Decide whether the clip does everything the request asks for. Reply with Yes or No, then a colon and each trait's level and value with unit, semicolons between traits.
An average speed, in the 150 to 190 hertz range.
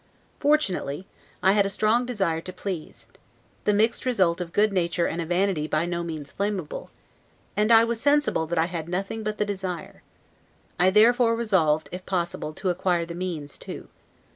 Yes: average, 170 wpm; medium, 185 Hz